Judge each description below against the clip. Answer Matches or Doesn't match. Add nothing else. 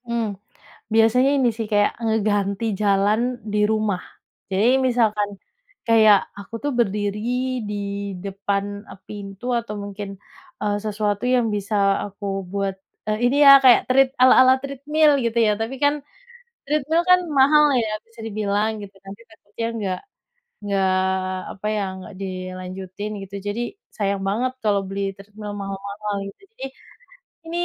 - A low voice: Doesn't match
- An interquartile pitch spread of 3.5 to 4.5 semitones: Doesn't match